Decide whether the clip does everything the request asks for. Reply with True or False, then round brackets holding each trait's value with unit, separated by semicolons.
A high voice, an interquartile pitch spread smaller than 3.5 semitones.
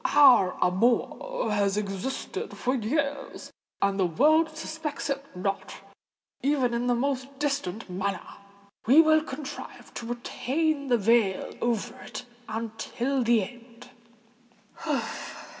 False (240 Hz; 5.3 semitones)